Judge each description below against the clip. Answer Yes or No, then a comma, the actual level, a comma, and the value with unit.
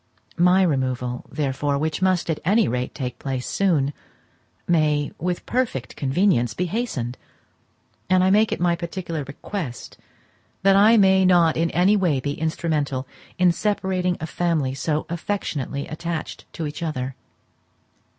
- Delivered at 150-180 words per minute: No, average, 140 wpm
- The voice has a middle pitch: Yes, medium, 165 Hz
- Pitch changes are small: No, average, 5.0 semitones